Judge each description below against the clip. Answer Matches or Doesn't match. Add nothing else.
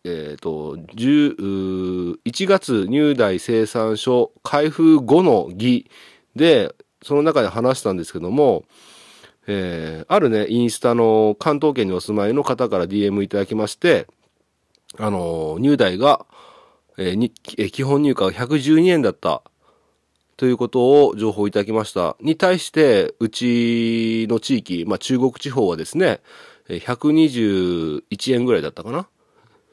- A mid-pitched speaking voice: Doesn't match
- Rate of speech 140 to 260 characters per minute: Matches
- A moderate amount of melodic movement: Doesn't match